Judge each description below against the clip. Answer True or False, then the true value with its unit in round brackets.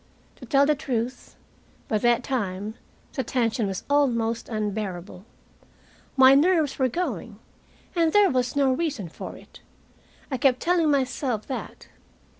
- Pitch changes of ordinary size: True (4.5 semitones)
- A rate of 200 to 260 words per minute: False (135 wpm)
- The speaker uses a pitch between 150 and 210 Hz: False (255 Hz)